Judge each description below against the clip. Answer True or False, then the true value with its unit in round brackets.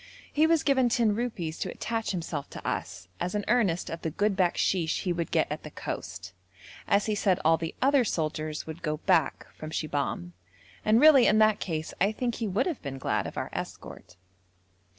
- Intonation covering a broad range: True (6.2 semitones)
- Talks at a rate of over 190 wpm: True (200 wpm)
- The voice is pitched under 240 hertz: True (185 Hz)